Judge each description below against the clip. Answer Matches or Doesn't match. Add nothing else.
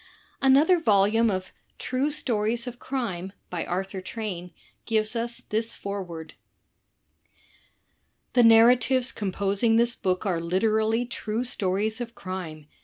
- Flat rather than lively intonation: Doesn't match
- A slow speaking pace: Matches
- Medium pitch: Doesn't match